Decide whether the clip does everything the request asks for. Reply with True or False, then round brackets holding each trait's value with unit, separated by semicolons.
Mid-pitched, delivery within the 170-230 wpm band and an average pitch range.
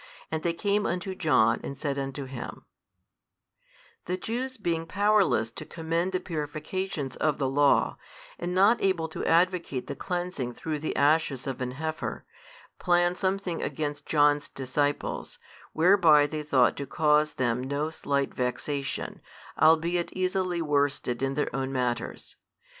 False (155 Hz; 140 wpm; 4.2 semitones)